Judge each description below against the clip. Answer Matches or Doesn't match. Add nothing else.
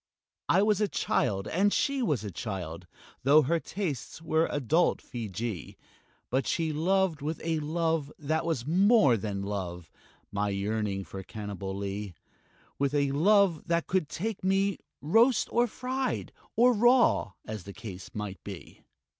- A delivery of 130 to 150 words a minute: Matches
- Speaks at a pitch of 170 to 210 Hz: Doesn't match